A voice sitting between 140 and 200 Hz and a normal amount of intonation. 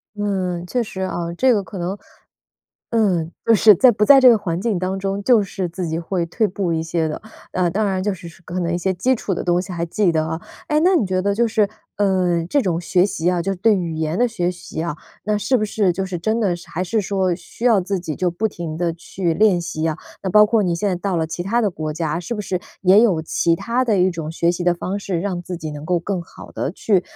Yes: medium, 185 Hz; average, 3.3 semitones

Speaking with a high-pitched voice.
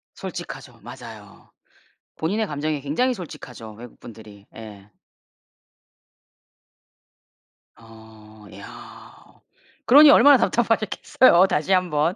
No: medium, 150 Hz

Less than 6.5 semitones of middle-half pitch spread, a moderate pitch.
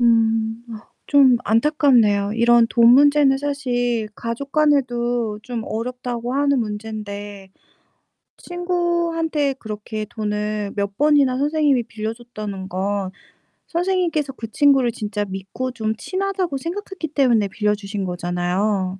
No: average, 5.2 semitones; high, 235 Hz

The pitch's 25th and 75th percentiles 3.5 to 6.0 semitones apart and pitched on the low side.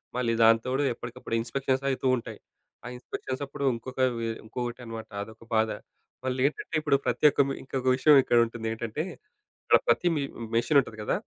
No: average, 2.9 semitones; low, 125 Hz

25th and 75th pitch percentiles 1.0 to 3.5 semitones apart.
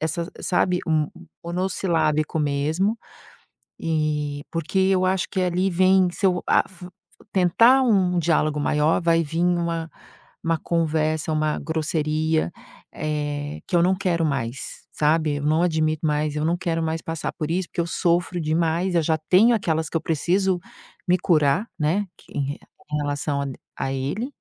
Yes: average, 2.8 semitones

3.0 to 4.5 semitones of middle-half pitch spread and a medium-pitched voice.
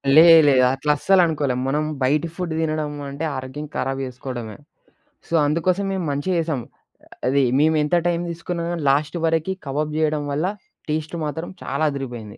Yes: average, 3.3 semitones; medium, 150 Hz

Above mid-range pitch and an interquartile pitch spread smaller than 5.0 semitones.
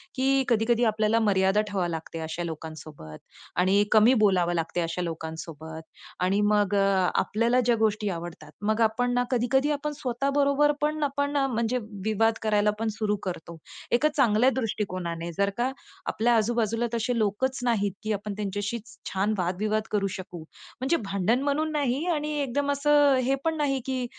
No: high, 220 Hz; wide, 5.4 semitones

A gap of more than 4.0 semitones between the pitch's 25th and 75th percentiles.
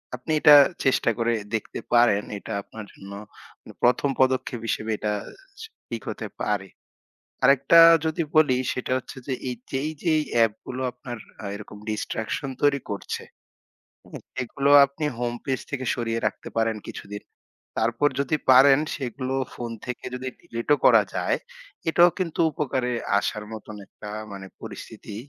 No: average, 3.7 semitones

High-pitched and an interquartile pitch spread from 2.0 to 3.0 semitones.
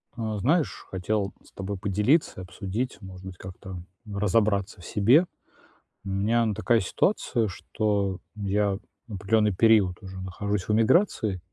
No: low, 105 Hz; average, 2.7 semitones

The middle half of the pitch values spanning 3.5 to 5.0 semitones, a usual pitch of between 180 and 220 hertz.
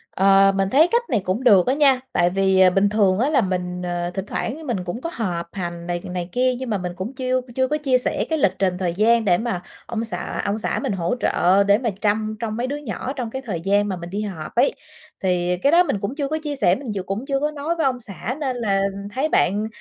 No: wide, 5.6 semitones; high, 210 Hz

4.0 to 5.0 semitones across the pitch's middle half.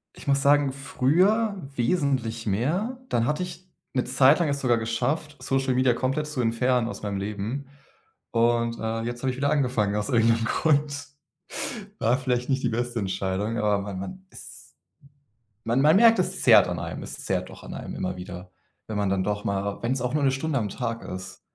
Yes: average, 4.4 semitones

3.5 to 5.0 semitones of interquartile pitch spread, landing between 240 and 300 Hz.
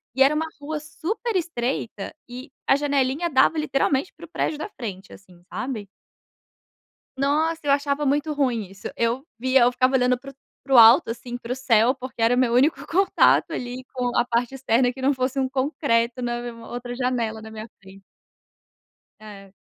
No: average, 3.1 semitones; very high, 255 Hz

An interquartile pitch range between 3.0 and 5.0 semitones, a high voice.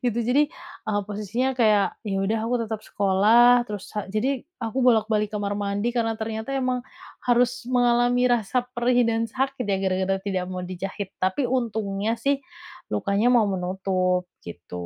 Yes: average, 3.7 semitones; high, 215 Hz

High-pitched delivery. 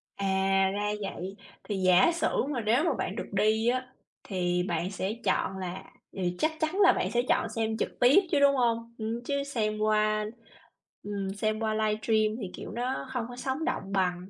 Yes: high, 215 Hz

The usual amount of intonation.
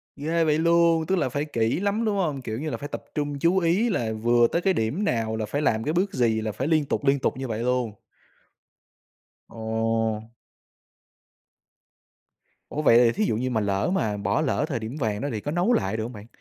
No: wide, 6.5 semitones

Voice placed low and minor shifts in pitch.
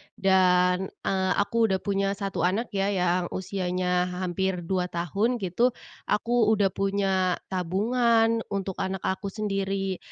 No: high, 190 Hz; narrow, 1.9 semitones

